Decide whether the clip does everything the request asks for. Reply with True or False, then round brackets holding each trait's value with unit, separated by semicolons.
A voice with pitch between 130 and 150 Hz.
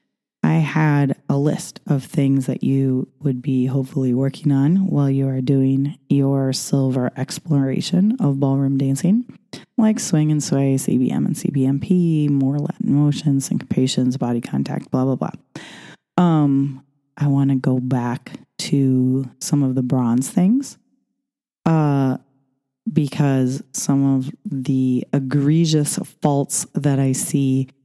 True (140 Hz)